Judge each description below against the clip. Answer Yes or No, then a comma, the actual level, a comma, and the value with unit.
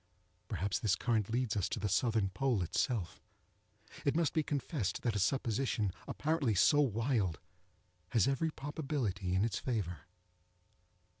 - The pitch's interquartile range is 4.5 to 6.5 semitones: Yes, wide, 5.6 semitones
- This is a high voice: No, low, 115 Hz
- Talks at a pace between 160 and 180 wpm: No, average, 140 wpm